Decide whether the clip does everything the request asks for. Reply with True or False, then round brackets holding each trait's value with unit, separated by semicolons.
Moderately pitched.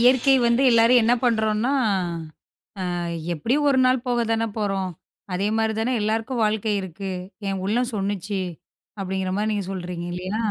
False (220 Hz)